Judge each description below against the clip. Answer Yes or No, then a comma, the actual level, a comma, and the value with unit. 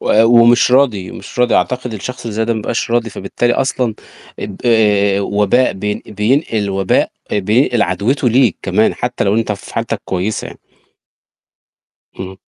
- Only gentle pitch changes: No, average, 3.2 semitones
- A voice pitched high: No, low, 110 Hz